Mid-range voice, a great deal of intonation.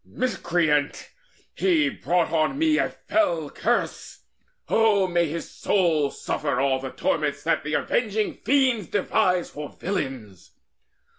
Yes: medium, 175 Hz; wide, 6.7 semitones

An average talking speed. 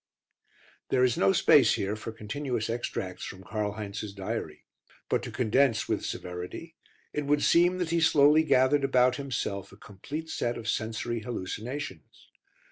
Yes: average, 150 wpm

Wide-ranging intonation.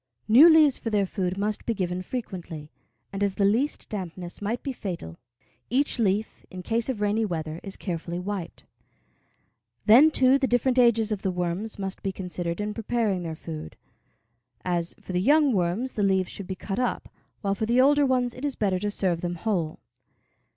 No: average, 4.7 semitones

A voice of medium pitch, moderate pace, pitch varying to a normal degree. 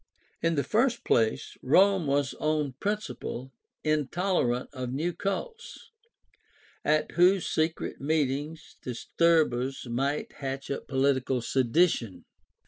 No: medium, 145 Hz; slow, 105 wpm; average, 4.3 semitones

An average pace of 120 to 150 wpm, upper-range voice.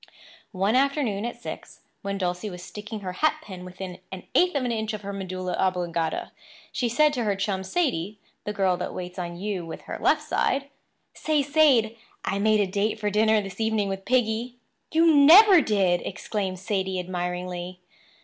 No: average, 180 wpm; high, 205 Hz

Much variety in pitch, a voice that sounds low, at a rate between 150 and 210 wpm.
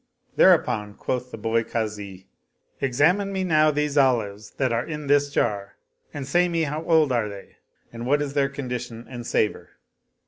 No: average, 4.7 semitones; low, 130 Hz; average, 175 wpm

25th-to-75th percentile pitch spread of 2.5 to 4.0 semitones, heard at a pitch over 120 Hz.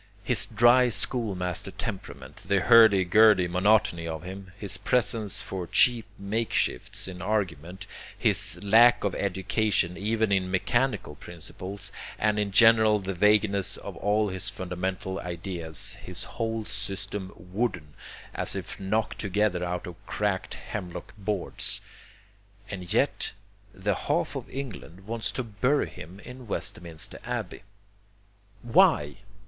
No: average, 3.2 semitones; low, 100 Hz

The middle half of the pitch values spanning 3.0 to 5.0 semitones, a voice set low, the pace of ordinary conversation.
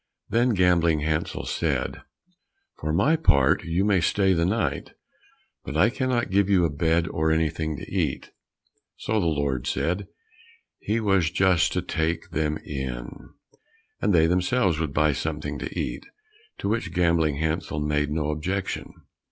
Yes: average, 3.8 semitones; very low, 80 Hz; average, 150 wpm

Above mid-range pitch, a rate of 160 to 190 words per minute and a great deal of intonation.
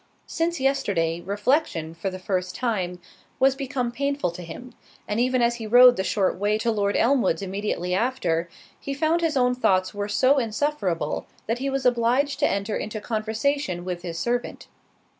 Yes: high, 225 Hz; average, 175 wpm; wide, 5.9 semitones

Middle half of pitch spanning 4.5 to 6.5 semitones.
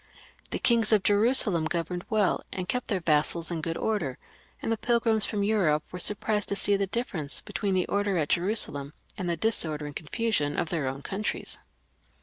Yes: average, 5.2 semitones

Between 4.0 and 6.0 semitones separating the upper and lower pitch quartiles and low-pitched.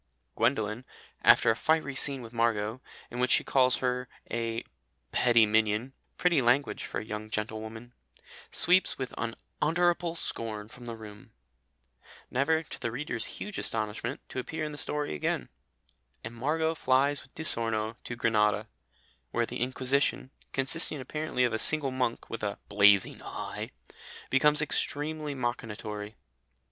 Yes: average, 4.3 semitones; low, 120 Hz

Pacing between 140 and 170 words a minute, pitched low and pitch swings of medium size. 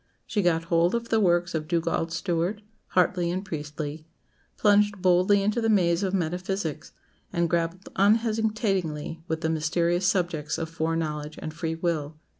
No: average, 155 wpm; medium, 175 Hz; average, 3.2 semitones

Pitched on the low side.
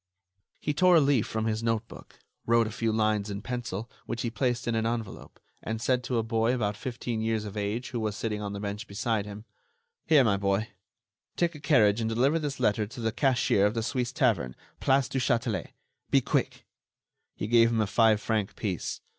Yes: low, 115 Hz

